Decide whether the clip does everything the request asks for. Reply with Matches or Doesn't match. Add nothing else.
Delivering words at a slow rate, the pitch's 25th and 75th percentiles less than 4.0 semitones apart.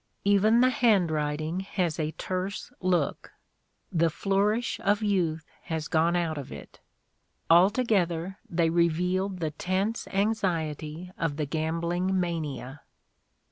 Matches